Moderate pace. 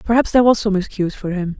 No: fast, 265 wpm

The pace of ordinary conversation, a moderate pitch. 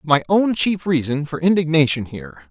Yes: average, 170 wpm; medium, 155 Hz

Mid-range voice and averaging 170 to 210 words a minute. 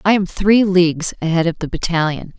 Yes: medium, 175 Hz; average, 200 wpm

